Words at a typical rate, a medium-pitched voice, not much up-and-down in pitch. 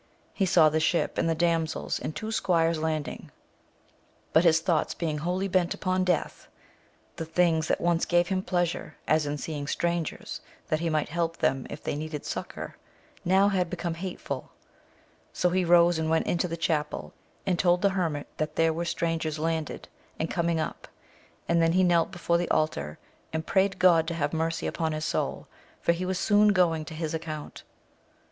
Yes: average, 185 wpm; medium, 165 Hz; narrow, 1.9 semitones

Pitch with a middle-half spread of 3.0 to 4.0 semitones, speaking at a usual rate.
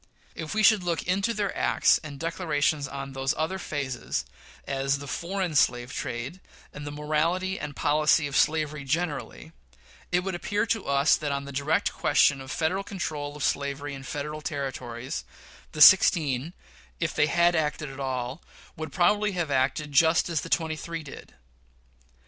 Yes: average, 3.6 semitones; average, 165 wpm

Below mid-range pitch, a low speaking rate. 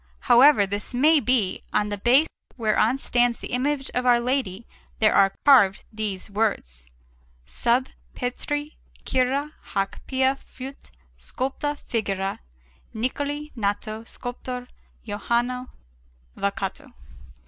No: high, 245 Hz; slow, 110 wpm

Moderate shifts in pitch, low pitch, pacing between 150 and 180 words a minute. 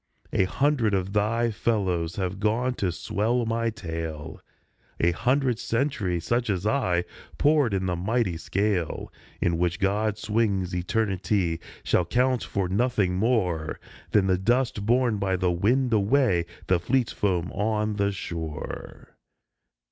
No: average, 4.4 semitones; low, 100 Hz; average, 140 wpm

